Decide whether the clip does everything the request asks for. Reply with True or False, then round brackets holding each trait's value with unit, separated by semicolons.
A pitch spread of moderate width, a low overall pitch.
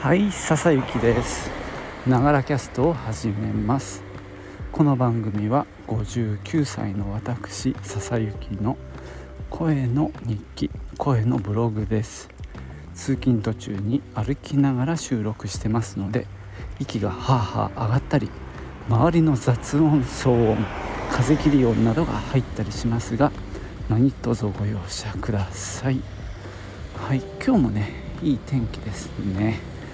True (4.8 semitones; 110 Hz)